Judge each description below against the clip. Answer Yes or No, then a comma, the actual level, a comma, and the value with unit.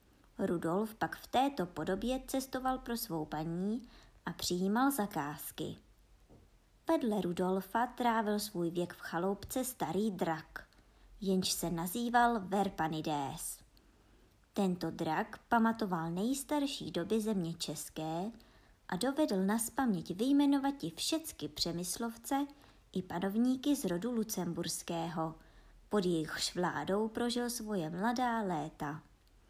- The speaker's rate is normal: No, slow, 105 wpm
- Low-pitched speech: No, high, 195 Hz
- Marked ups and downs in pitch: Yes, wide, 6.2 semitones